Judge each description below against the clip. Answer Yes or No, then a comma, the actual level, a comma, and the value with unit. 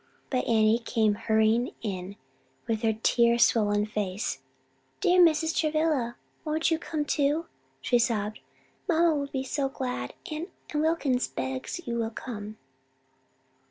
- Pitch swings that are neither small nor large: No, wide, 6.0 semitones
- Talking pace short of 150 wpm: Yes, slow, 135 wpm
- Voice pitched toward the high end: Yes, high, 240 Hz